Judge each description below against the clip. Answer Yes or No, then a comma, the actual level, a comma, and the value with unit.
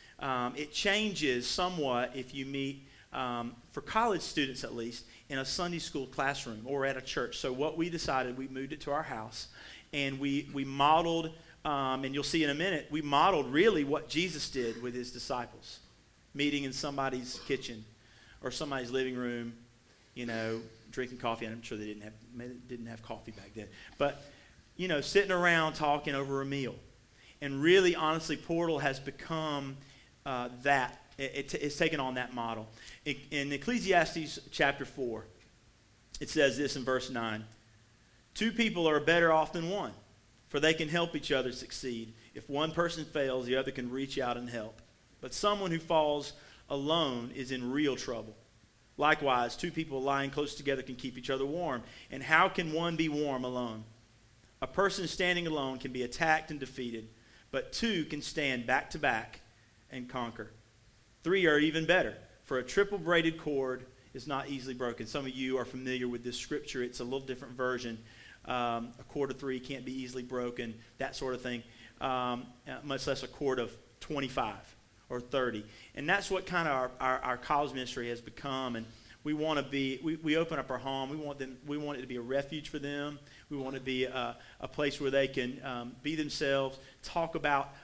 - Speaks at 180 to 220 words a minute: Yes, average, 190 wpm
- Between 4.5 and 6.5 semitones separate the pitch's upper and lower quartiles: No, average, 3.5 semitones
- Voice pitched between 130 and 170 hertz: Yes, low, 135 Hz